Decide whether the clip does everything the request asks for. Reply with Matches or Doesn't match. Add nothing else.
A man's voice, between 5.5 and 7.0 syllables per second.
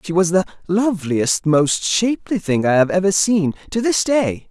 Doesn't match